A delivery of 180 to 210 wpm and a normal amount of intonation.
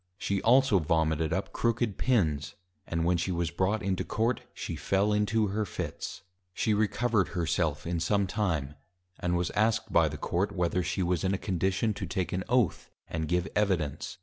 Yes: average, 190 wpm; average, 3.8 semitones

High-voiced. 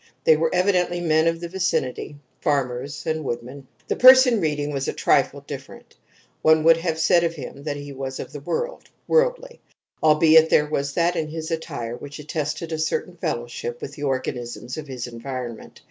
No: medium, 155 Hz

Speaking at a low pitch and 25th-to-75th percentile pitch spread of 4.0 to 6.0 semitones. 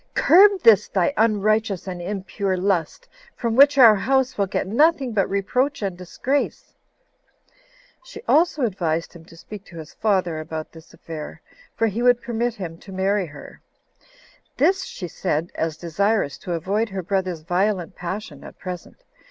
No: high, 195 Hz; average, 5.0 semitones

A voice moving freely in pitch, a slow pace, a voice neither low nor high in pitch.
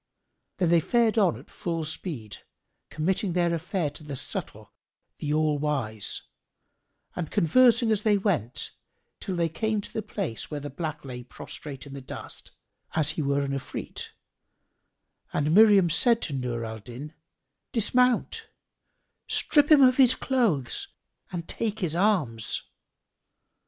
No: wide, 7.0 semitones; average, 145 wpm; medium, 165 Hz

